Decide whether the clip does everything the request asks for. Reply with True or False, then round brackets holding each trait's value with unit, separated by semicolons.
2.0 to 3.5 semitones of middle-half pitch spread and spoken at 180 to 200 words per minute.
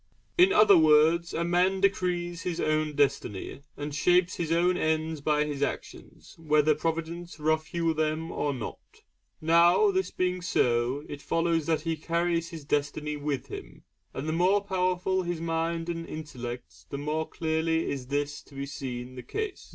False (3.0 semitones; 165 wpm)